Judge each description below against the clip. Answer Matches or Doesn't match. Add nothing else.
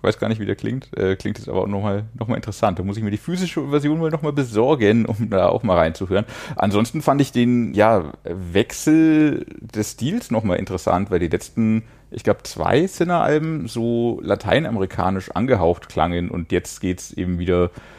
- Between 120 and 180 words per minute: Doesn't match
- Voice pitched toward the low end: Matches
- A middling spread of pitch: Doesn't match